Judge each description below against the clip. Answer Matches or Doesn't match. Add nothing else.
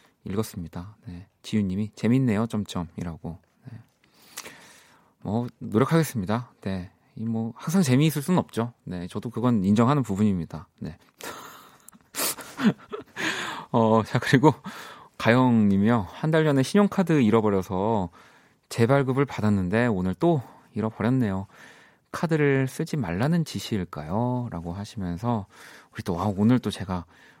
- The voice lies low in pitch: Matches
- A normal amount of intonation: Matches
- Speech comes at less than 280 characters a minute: Matches